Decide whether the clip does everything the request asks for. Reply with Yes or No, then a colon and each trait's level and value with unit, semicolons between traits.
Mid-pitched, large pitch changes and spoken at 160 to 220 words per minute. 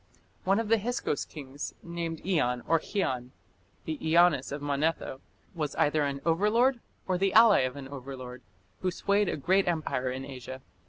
Yes: medium, 160 Hz; wide, 5.9 semitones; average, 165 wpm